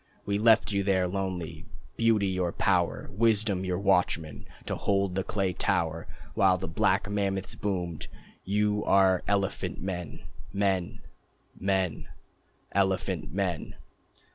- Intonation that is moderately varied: No, narrow, 1.8 semitones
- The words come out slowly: Yes, slow, 120 wpm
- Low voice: Yes, very low, 95 Hz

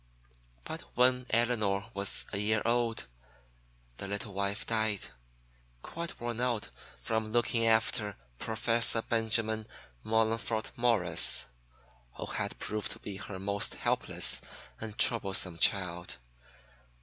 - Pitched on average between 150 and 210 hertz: No, low, 110 Hz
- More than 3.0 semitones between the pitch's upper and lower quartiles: No, narrow, 2.4 semitones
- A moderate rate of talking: No, slow, 115 wpm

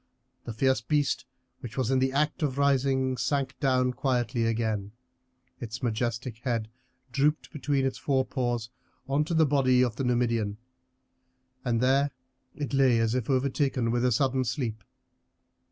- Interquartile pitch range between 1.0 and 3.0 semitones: Yes, narrow, 2.6 semitones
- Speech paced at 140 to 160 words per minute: Yes, average, 150 wpm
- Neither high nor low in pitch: No, low, 130 Hz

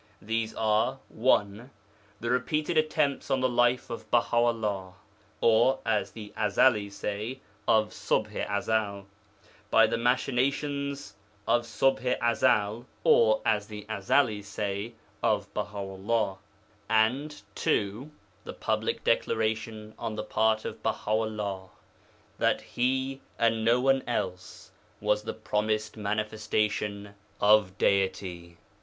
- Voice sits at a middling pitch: No, low, 110 Hz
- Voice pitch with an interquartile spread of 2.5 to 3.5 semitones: Yes, average, 2.8 semitones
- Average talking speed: No, slow, 125 wpm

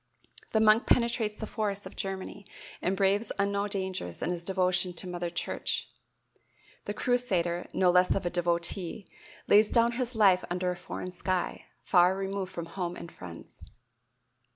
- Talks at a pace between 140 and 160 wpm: Yes, average, 155 wpm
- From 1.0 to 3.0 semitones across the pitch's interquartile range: Yes, narrow, 2.6 semitones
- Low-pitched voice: No, high, 190 Hz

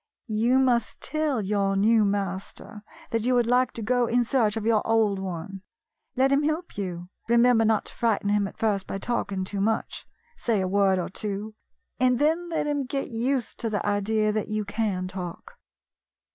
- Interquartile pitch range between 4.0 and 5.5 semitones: No, average, 3.6 semitones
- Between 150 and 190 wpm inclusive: Yes, average, 185 wpm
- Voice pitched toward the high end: Yes, high, 220 Hz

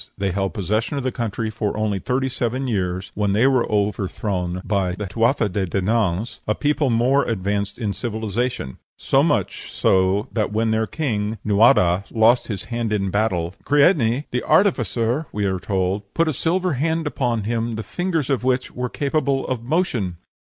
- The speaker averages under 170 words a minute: No, average, 175 wpm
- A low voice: Yes, low, 110 Hz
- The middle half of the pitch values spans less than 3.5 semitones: No, average, 4.3 semitones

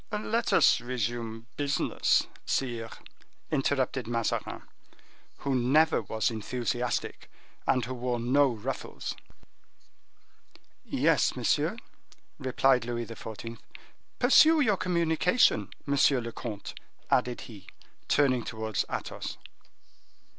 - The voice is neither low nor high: No, low, 125 Hz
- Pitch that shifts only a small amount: No, average, 3.6 semitones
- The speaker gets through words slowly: Yes, slow, 95 wpm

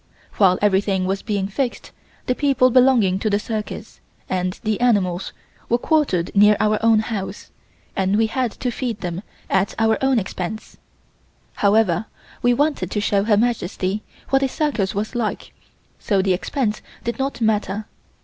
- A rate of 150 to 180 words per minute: Yes, average, 160 wpm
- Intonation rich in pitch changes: No, average, 3.8 semitones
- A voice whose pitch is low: No, high, 215 Hz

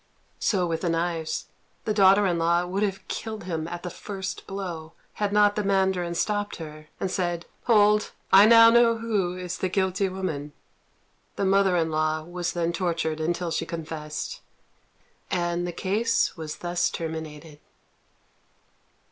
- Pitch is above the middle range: No, medium, 180 Hz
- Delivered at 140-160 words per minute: Yes, average, 155 wpm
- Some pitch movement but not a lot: Yes, average, 3.1 semitones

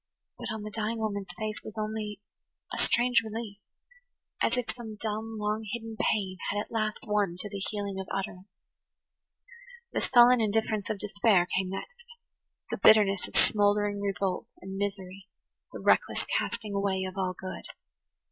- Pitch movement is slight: Yes, narrow, 2.0 semitones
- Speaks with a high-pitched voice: Yes, high, 210 Hz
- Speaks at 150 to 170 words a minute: Yes, average, 155 wpm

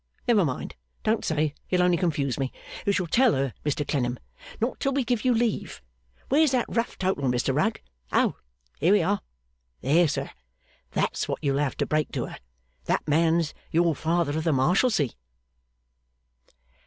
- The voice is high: No, medium, 165 Hz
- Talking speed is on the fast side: No, average, 165 wpm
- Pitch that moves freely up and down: Yes, wide, 6.6 semitones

